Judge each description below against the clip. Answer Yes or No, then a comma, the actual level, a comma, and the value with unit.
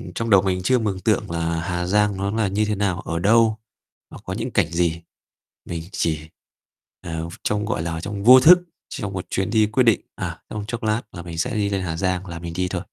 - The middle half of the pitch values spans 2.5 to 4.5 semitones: Yes, average, 3.9 semitones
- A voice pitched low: Yes, very low, 95 Hz